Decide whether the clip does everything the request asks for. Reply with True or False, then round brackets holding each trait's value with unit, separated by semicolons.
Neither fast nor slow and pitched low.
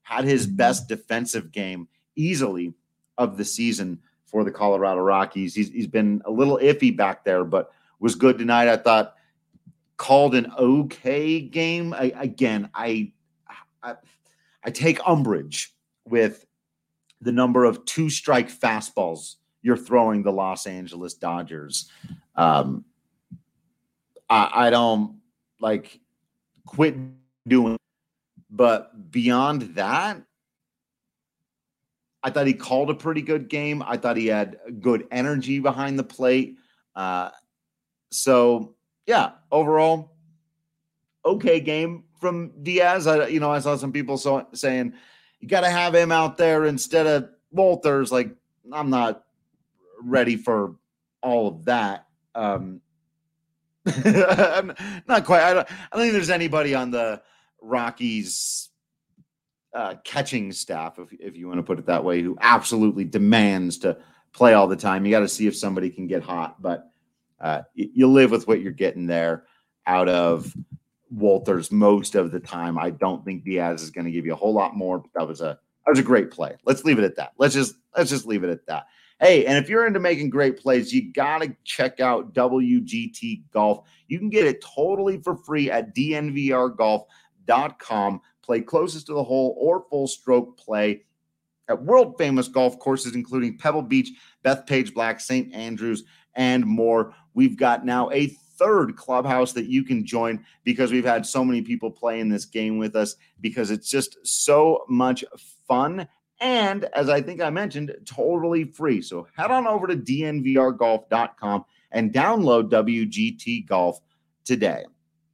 True (155 wpm; 125 Hz)